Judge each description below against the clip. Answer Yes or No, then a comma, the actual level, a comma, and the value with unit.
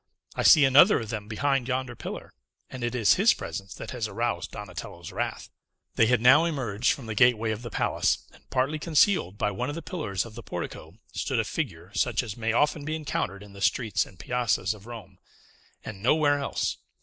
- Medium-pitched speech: No, low, 120 Hz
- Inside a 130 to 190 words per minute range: No, fast, 205 wpm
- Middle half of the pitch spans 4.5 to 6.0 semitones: Yes, average, 5.0 semitones